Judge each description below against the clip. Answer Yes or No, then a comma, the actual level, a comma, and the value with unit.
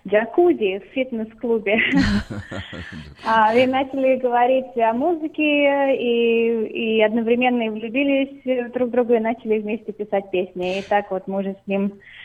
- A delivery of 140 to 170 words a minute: No, average, 125 wpm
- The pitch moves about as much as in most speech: Yes, average, 4.2 semitones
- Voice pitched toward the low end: No, high, 225 Hz